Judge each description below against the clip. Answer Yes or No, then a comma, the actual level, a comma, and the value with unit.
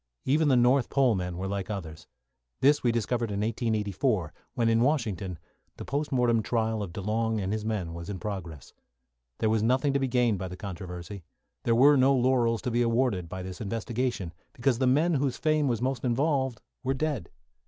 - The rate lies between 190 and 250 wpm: Yes, average, 195 wpm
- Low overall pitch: Yes, low, 115 Hz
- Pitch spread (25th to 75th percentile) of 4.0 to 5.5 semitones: Yes, average, 4.6 semitones